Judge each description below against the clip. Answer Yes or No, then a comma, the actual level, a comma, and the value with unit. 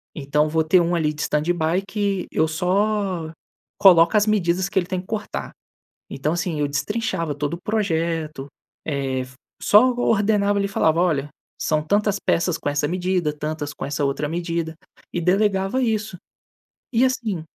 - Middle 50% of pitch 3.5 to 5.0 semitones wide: Yes, average, 4.5 semitones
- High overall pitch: No, medium, 175 Hz